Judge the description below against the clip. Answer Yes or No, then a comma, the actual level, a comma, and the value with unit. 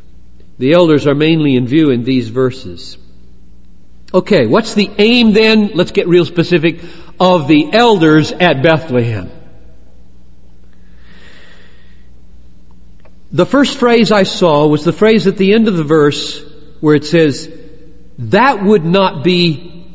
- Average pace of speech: No, slow, 130 wpm